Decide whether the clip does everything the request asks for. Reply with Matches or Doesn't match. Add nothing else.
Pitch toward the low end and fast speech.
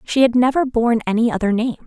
Doesn't match